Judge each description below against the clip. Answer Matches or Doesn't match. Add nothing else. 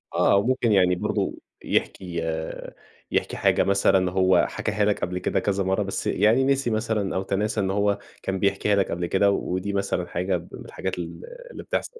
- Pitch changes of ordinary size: Doesn't match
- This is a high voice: Doesn't match